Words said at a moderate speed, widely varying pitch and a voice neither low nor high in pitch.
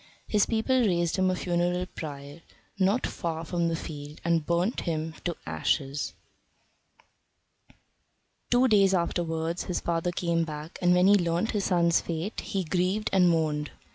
No: average, 155 wpm; narrow, 2.5 semitones; medium, 175 Hz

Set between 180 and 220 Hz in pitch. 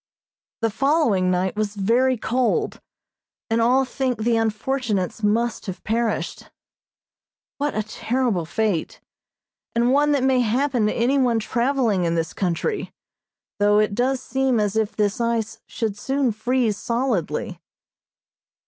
No: high, 230 Hz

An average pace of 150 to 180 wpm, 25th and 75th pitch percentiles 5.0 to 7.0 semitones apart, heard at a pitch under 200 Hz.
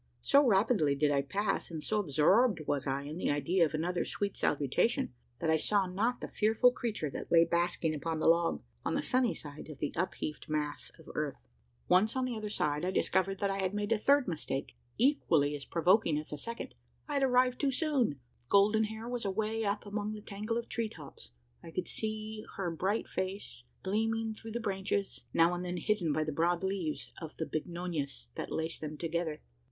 No: fast, 205 wpm; wide, 5.6 semitones; high, 190 Hz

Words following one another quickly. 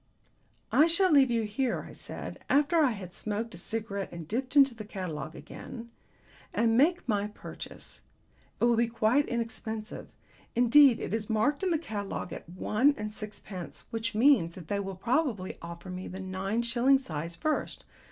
No: average, 175 wpm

